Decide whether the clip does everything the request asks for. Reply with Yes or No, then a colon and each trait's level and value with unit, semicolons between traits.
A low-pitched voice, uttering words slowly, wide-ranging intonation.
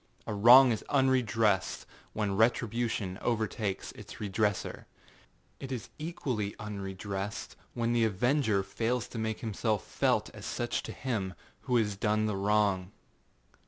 No: low, 110 Hz; slow, 130 wpm; average, 3.1 semitones